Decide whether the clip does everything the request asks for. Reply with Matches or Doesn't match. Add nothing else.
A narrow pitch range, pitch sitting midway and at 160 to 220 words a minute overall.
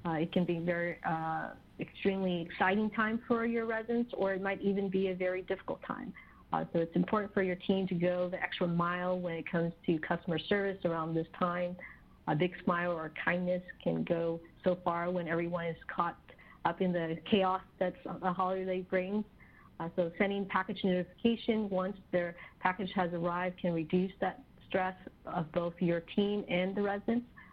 Matches